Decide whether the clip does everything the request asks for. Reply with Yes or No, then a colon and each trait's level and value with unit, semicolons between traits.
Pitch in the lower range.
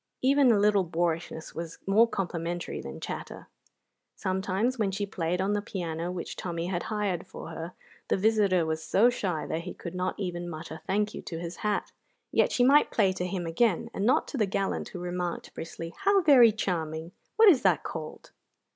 No: medium, 185 Hz